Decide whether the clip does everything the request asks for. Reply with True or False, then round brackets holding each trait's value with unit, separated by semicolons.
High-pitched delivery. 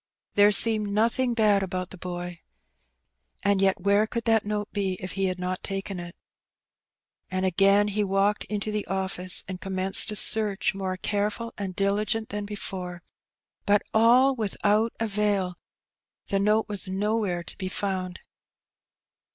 True (200 Hz)